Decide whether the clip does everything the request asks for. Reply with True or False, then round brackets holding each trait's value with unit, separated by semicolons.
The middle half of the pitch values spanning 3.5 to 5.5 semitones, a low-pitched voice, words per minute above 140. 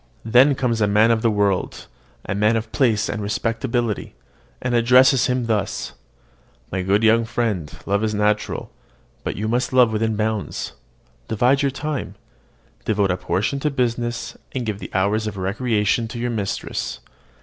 False (2.7 semitones; 110 Hz; 160 wpm)